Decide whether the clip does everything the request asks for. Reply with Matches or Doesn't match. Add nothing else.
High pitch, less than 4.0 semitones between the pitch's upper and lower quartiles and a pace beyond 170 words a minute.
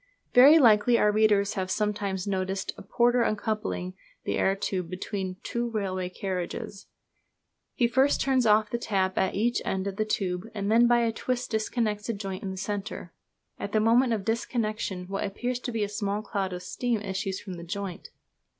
Matches